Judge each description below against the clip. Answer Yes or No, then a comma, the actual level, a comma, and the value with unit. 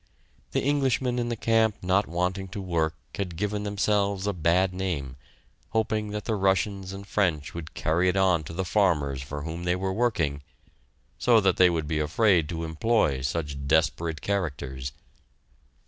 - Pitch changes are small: No, average, 4.2 semitones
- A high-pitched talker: No, very low, 90 Hz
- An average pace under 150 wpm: No, average, 165 wpm